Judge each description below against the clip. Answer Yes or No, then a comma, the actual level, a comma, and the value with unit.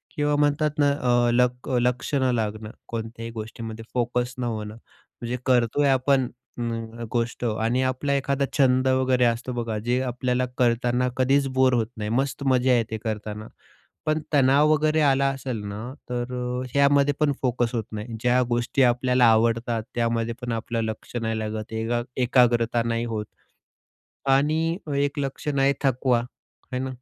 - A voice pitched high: No, low, 125 Hz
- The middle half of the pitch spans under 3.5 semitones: Yes, narrow, 2.6 semitones